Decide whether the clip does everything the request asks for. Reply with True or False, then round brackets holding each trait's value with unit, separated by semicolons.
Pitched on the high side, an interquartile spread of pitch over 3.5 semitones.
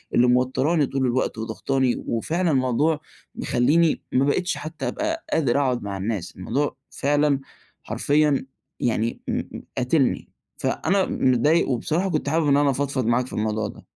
False (135 Hz; 3.9 semitones)